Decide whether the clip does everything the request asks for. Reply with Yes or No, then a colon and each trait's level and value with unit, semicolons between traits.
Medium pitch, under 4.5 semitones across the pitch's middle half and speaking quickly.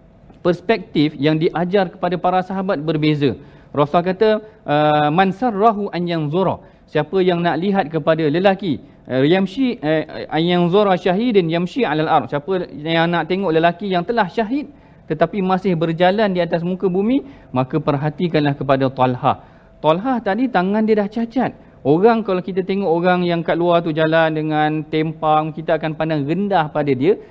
Yes: medium, 175 Hz; average, 3.9 semitones; fast, 160 wpm